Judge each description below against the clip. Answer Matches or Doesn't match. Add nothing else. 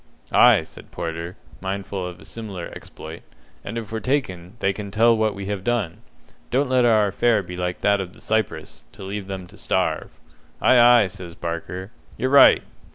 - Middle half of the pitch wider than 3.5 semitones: Matches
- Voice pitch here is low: Matches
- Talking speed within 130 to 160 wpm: Doesn't match